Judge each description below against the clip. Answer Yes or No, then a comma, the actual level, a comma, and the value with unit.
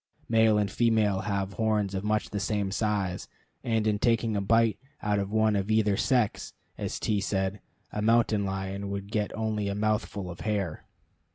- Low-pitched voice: Yes, low, 105 Hz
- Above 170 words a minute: Yes, average, 180 wpm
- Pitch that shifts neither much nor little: No, narrow, 1.8 semitones